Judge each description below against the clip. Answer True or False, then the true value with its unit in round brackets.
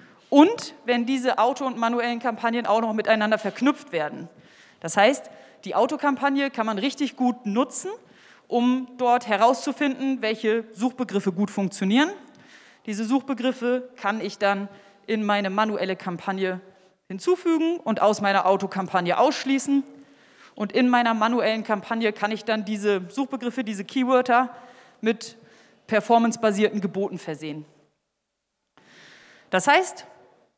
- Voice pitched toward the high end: True (230 Hz)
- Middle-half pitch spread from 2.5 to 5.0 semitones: True (4.1 semitones)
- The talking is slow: True (120 wpm)